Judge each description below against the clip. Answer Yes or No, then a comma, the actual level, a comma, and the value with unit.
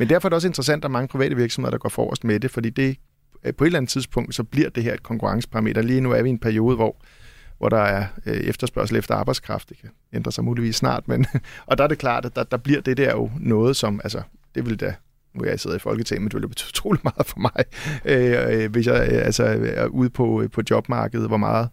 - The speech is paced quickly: Yes, fast, 260 wpm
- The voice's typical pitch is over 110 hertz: Yes, low, 120 Hz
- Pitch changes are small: No, average, 3.1 semitones